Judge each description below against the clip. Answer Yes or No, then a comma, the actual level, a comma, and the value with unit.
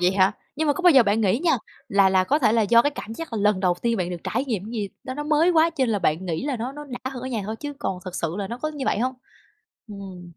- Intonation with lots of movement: Yes, wide, 6.2 semitones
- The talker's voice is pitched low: No, high, 230 Hz